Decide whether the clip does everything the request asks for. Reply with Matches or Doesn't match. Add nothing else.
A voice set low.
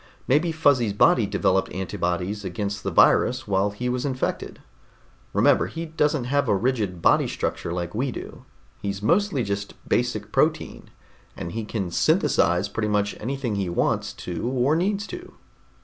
Matches